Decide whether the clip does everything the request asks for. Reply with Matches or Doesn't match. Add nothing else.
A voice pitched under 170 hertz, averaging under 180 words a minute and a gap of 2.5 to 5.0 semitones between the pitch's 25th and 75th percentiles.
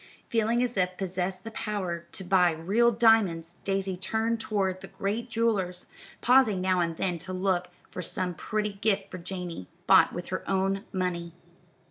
Doesn't match